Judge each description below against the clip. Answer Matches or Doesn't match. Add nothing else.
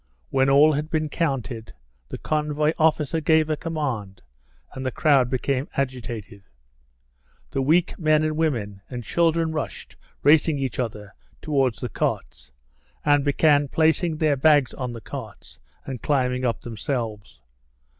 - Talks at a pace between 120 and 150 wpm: Matches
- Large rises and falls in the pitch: Doesn't match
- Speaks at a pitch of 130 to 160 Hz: Matches